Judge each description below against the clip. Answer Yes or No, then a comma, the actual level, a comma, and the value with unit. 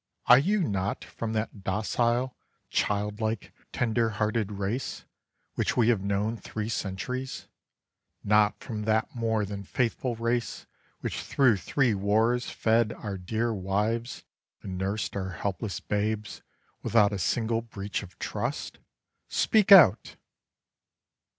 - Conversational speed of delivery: No, slow, 125 wpm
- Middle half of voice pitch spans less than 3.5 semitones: Yes, narrow, 2.5 semitones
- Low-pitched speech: Yes, low, 110 Hz